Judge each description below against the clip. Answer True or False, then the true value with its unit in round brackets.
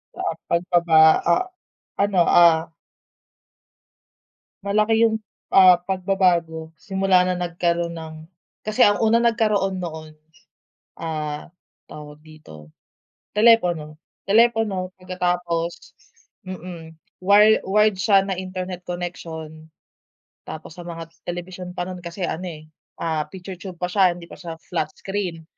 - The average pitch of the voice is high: False (180 Hz)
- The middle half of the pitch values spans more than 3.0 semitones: False (2.7 semitones)